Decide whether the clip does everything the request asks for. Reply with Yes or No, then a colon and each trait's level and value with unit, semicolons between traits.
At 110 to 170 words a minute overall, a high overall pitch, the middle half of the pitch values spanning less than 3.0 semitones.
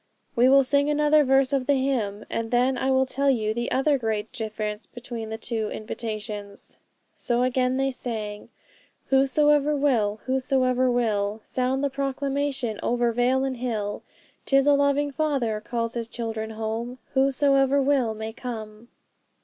No: average, 150 wpm; very high, 250 Hz; average, 3.6 semitones